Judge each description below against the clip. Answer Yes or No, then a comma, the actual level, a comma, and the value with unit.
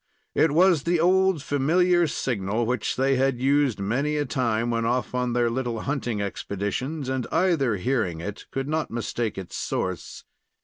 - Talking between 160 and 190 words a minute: Yes, average, 165 wpm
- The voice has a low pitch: Yes, low, 130 Hz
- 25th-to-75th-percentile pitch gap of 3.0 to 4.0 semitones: No, average, 4.4 semitones